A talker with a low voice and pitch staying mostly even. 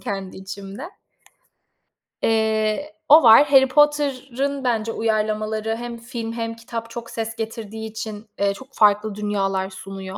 No: high, 225 Hz; narrow, 2.3 semitones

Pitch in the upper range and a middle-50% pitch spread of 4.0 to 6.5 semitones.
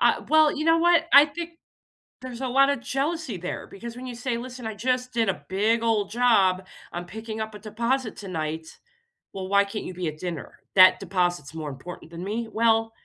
Yes: high, 220 Hz; wide, 5.4 semitones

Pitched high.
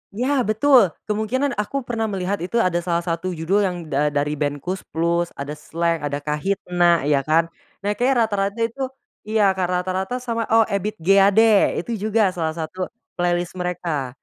No: medium, 180 Hz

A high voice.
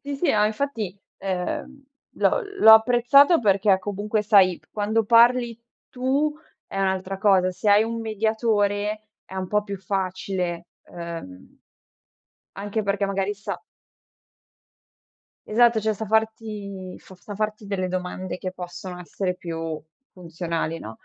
Yes: high, 205 Hz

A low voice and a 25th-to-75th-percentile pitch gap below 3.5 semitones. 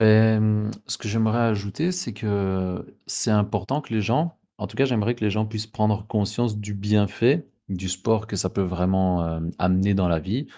Yes: low, 105 Hz; average, 2.7 semitones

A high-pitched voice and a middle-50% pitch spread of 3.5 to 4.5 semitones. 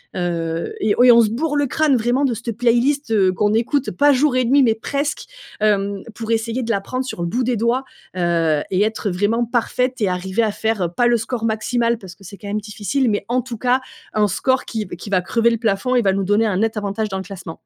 Yes: high, 225 Hz; average, 3.8 semitones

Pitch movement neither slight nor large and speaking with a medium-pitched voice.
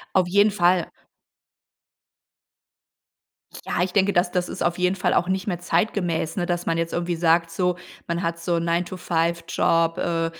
No: narrow, 1.3 semitones; medium, 175 Hz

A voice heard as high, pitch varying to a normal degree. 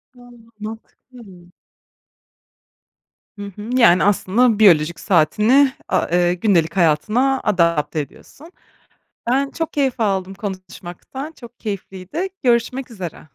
No: high, 210 Hz; wide, 5.9 semitones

